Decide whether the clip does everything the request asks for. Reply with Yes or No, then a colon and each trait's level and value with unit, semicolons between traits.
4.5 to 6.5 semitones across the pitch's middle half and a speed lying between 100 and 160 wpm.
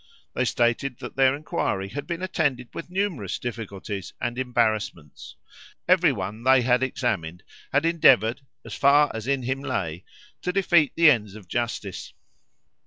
Yes: average, 5.0 semitones; average, 150 wpm